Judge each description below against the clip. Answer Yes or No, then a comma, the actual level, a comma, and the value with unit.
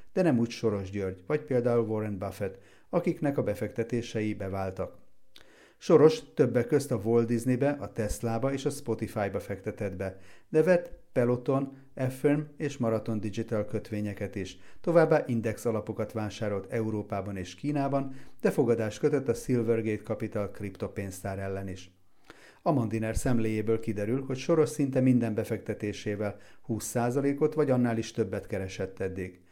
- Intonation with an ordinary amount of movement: Yes, average, 4.3 semitones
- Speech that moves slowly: No, average, 135 wpm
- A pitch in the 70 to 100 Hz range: No, low, 110 Hz